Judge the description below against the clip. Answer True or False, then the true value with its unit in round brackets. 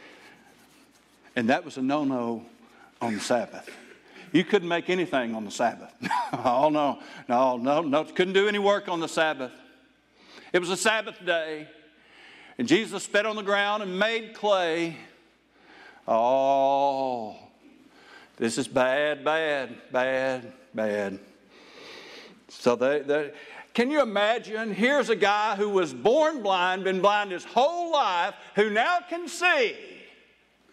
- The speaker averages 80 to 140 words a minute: True (135 wpm)